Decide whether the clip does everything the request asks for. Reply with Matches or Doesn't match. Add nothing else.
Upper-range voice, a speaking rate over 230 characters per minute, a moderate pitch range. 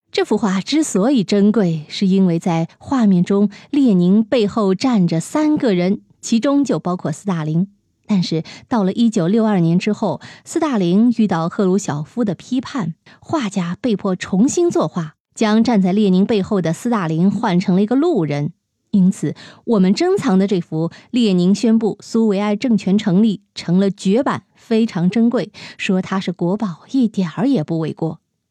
Matches